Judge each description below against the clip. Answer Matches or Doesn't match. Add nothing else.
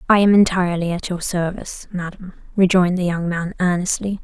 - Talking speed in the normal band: Matches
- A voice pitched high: Doesn't match